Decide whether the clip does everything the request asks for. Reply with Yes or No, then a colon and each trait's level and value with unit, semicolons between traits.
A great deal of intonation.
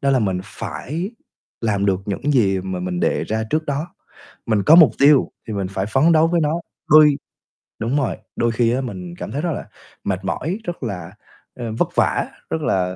Yes: wide, 7.6 semitones